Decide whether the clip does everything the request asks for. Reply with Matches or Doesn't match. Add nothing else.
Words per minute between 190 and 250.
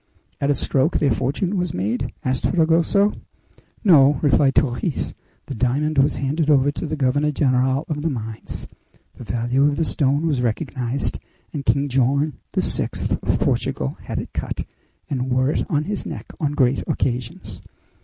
Doesn't match